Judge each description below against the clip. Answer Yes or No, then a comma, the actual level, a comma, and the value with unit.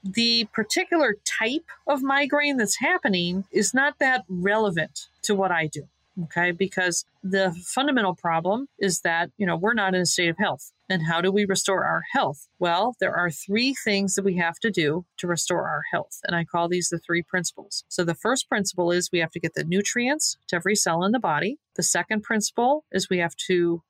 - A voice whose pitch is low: No, high, 190 Hz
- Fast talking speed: Yes, fast, 210 wpm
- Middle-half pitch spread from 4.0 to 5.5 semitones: Yes, average, 4.6 semitones